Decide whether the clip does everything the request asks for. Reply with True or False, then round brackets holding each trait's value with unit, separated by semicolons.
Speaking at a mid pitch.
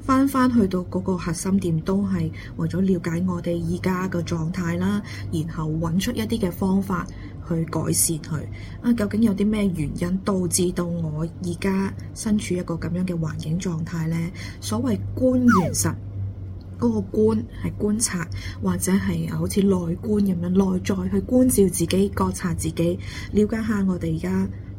True (170 Hz)